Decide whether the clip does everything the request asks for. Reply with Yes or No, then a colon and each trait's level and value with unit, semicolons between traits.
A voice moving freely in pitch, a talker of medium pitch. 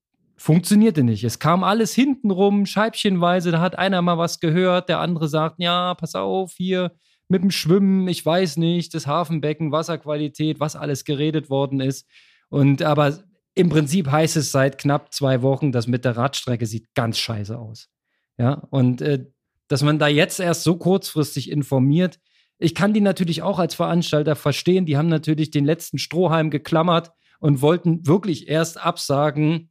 No: average, 3.6 semitones; medium, 160 Hz